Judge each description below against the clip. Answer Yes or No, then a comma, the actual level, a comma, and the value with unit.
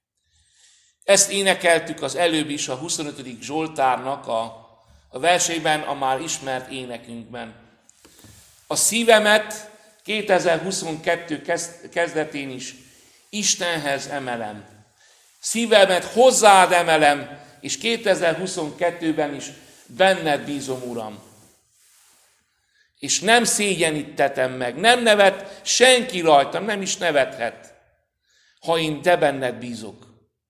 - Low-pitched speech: No, medium, 160 Hz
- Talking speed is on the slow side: Yes, slow, 90 wpm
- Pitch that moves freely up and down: Yes, wide, 5.9 semitones